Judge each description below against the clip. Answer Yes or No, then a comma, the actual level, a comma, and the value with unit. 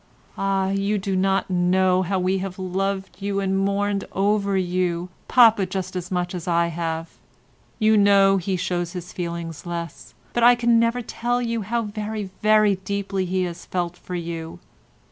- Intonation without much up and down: Yes, narrow, 2.3 semitones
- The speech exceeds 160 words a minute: Yes, average, 170 wpm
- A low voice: No, high, 190 Hz